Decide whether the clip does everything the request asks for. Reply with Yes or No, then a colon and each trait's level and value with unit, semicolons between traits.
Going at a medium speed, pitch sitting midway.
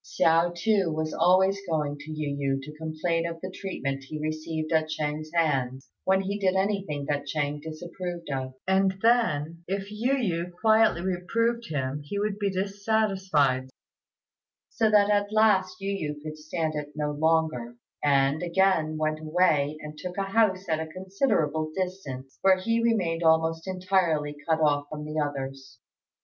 Yes: average, 160 wpm; medium, 165 Hz